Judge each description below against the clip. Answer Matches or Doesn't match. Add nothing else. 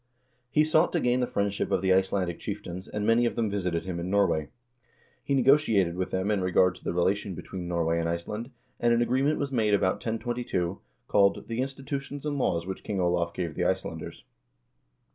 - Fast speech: Doesn't match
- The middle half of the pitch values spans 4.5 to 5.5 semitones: Matches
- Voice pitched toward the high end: Doesn't match